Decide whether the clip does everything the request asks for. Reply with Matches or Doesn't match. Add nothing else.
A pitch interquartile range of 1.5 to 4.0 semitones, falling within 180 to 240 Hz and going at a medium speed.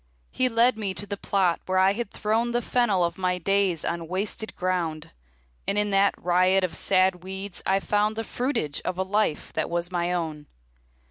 Matches